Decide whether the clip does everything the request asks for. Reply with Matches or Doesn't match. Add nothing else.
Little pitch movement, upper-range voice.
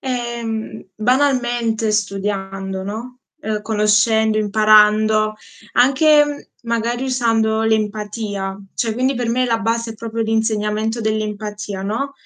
Matches